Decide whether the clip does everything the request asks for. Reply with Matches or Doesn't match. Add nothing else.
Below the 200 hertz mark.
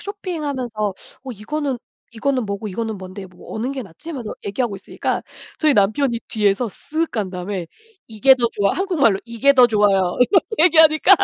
Doesn't match